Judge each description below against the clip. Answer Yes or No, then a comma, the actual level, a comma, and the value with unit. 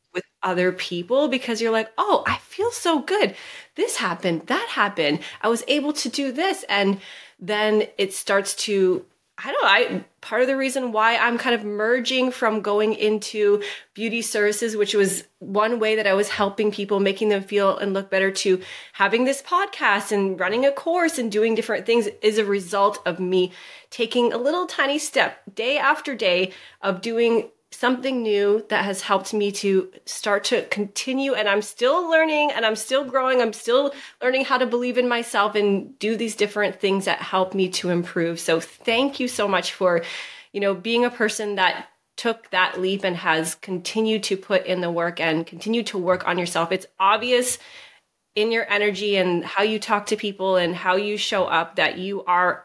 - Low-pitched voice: No, high, 210 Hz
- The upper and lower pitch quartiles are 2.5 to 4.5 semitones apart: Yes, average, 4.1 semitones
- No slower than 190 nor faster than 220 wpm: Yes, average, 195 wpm